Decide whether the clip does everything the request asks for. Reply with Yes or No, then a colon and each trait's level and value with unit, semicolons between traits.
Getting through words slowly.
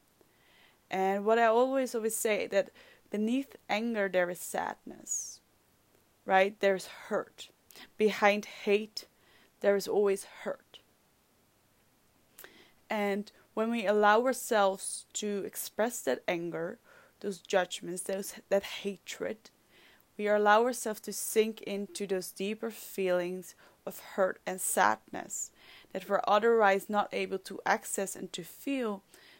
Yes: slow, 120 wpm